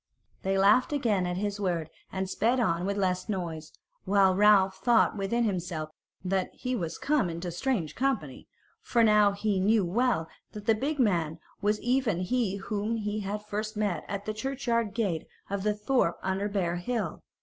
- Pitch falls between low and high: No, high, 205 Hz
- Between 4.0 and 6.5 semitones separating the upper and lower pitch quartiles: No, average, 3.5 semitones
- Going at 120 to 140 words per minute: No, average, 175 wpm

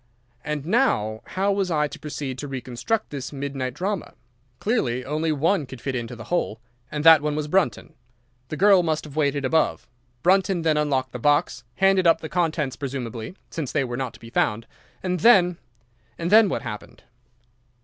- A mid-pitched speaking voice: Yes, medium, 150 Hz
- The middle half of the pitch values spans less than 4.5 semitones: No, wide, 5.5 semitones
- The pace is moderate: Yes, average, 170 wpm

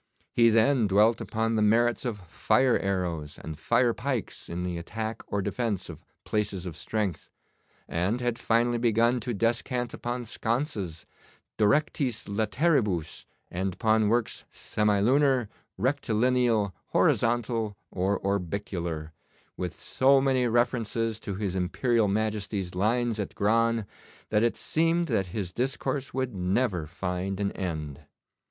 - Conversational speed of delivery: No, slow, 130 wpm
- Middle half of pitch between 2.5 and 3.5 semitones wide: No, average, 4.0 semitones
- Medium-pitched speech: No, low, 110 Hz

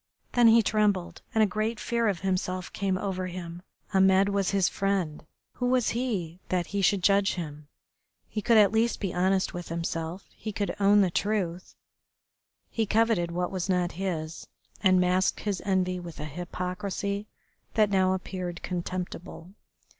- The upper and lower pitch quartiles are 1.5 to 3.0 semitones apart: Yes, narrow, 2.4 semitones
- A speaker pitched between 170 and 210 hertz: Yes, high, 190 Hz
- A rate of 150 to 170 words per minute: Yes, average, 160 wpm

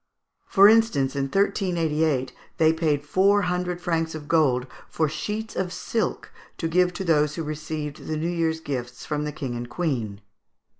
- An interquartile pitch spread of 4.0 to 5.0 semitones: No, average, 3.4 semitones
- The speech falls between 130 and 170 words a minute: Yes, average, 165 wpm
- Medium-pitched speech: Yes, medium, 160 Hz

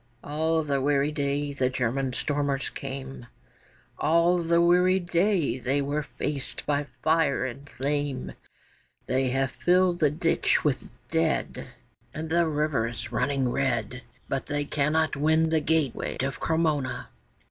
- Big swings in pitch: No, average, 3.0 semitones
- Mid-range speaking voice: Yes, medium, 145 Hz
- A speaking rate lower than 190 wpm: Yes, slow, 135 wpm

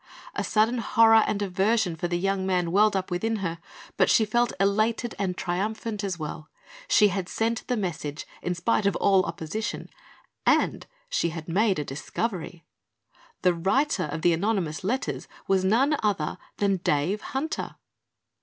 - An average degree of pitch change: Yes, average, 4.0 semitones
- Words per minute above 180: No, average, 160 wpm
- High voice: Yes, high, 195 Hz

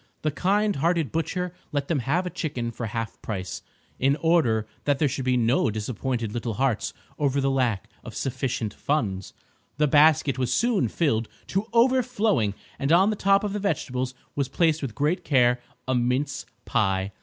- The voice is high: No, low, 135 Hz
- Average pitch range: No, wide, 6.0 semitones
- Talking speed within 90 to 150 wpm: No, average, 175 wpm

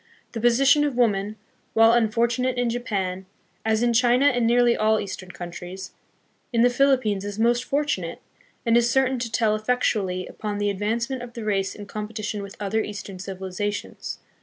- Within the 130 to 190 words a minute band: Yes, average, 170 wpm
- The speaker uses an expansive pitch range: No, average, 3.1 semitones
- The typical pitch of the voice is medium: No, high, 220 Hz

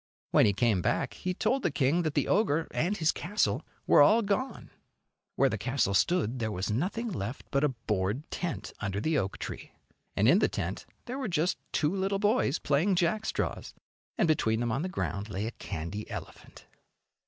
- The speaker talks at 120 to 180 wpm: No, average, 190 wpm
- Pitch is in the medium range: Yes, medium, 145 Hz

